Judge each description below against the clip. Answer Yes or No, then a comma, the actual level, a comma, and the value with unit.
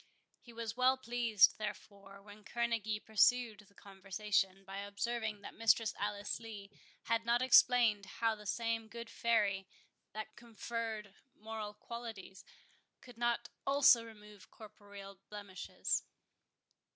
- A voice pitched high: Yes, high, 215 Hz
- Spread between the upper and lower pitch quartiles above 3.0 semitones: No, narrow, 2.4 semitones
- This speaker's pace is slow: Yes, slow, 120 wpm